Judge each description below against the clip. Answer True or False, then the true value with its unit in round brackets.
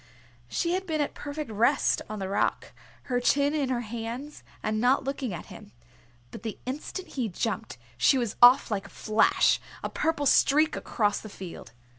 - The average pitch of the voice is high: True (245 Hz)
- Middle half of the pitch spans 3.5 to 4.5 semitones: False (5.0 semitones)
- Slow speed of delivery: False (180 wpm)